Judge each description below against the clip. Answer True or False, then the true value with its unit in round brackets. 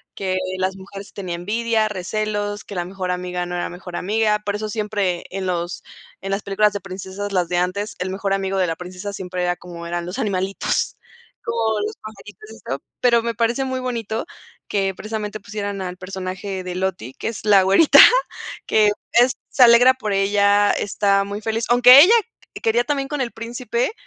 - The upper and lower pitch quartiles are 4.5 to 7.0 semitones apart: False (3.0 semitones)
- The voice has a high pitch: True (200 Hz)